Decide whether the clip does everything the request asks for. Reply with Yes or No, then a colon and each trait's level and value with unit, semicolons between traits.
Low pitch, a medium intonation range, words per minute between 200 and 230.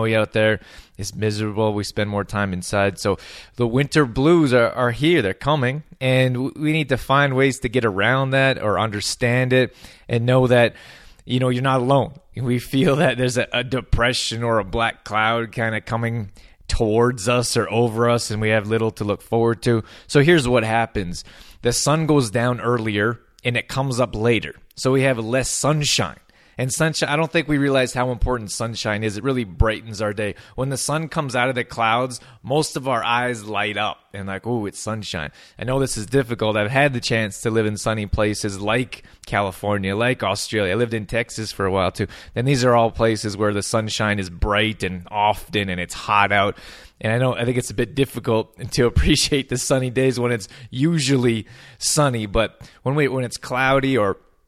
Yes: low, 120 Hz; average, 3.4 semitones; fast, 205 wpm